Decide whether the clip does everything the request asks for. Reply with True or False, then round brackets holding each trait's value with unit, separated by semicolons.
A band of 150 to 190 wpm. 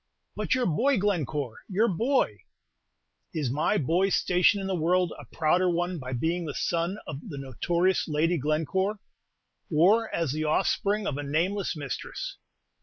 True (155 wpm)